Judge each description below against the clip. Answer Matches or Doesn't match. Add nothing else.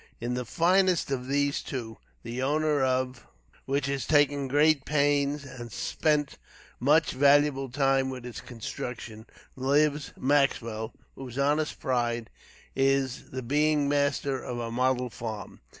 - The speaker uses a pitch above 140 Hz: Doesn't match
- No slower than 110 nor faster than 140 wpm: Matches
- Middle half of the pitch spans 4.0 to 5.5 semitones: Doesn't match